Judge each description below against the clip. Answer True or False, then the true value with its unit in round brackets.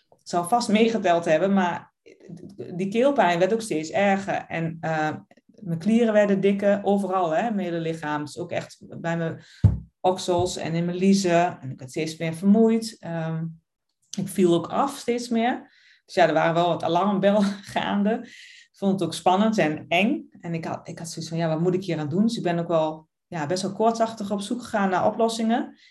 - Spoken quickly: True (205 wpm)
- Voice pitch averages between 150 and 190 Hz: True (185 Hz)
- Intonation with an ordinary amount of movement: True (4.9 semitones)